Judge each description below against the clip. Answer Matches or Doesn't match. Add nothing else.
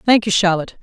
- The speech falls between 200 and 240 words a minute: Matches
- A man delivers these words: Doesn't match